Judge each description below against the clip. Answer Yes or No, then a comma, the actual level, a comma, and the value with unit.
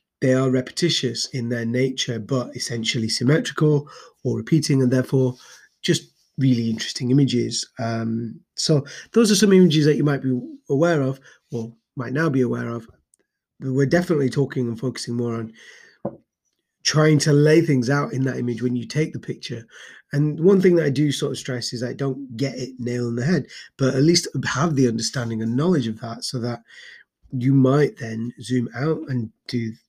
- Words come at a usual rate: Yes, average, 185 wpm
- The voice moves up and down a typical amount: Yes, average, 3.4 semitones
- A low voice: Yes, low, 130 Hz